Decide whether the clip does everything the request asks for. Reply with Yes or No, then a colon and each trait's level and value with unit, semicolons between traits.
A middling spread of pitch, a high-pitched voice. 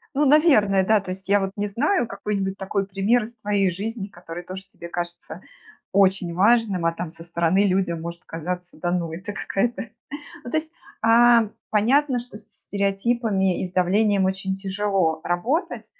Yes: average, 3.4 semitones; high, 195 Hz